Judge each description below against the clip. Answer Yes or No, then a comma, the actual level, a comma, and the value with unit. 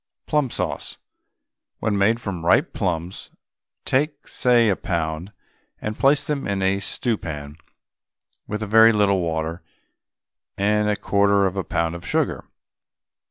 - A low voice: Yes, low, 100 Hz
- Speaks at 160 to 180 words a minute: No, average, 140 wpm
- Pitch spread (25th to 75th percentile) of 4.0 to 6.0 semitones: Yes, average, 4.5 semitones